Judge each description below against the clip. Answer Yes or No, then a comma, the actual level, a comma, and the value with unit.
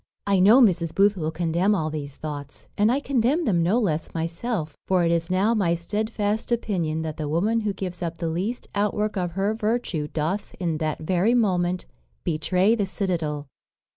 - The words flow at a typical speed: Yes, average, 185 wpm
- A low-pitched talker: No, medium, 185 Hz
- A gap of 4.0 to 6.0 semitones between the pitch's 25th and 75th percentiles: Yes, average, 4.4 semitones